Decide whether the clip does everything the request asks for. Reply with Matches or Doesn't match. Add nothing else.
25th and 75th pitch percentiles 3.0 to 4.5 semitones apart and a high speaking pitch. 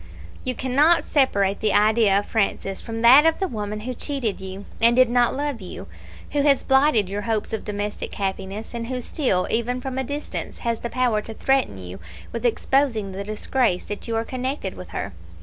Matches